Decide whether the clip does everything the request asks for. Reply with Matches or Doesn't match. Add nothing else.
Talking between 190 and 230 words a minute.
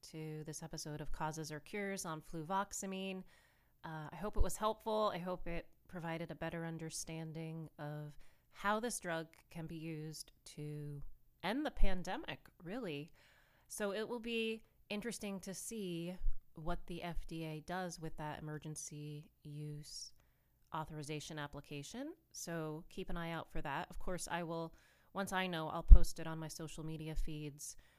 Doesn't match